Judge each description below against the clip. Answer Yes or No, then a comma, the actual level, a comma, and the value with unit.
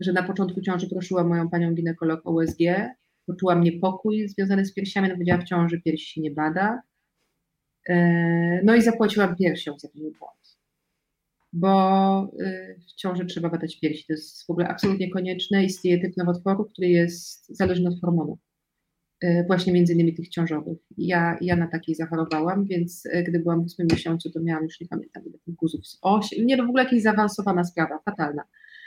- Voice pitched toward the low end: No, medium, 175 Hz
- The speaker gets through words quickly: Yes, fast, 170 wpm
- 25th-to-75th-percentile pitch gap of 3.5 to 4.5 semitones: No, narrow, 2.4 semitones